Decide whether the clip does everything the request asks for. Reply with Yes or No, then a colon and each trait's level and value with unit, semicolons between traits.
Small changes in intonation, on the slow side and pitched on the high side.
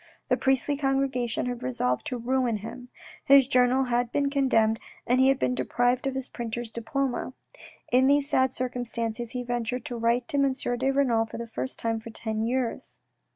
No: narrow, 2.3 semitones; average, 185 wpm; high, 245 Hz